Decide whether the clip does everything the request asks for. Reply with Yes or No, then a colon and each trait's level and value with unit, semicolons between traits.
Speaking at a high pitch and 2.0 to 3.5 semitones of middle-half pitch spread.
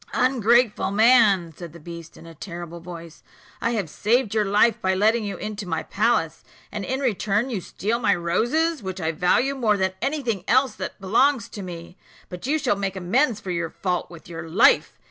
No: high, 200 Hz; average, 5.2 semitones